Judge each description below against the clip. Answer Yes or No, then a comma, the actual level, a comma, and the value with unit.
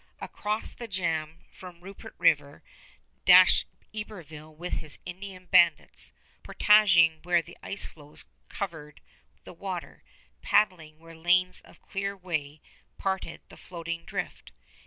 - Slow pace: Yes, slow, 120 wpm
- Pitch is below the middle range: No, medium, 175 Hz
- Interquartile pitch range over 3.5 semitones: No, average, 3.1 semitones